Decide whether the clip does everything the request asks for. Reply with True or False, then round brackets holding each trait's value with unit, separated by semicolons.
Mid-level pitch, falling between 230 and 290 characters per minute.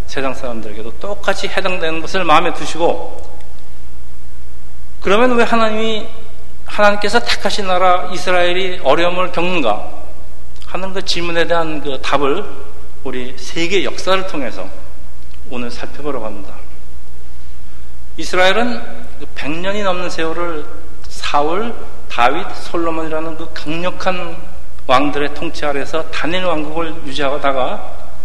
True (160 Hz; 270 characters per minute)